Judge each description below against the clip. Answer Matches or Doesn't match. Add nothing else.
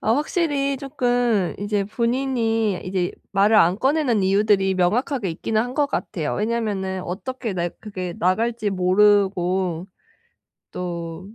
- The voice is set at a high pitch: Matches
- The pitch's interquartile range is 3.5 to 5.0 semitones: Matches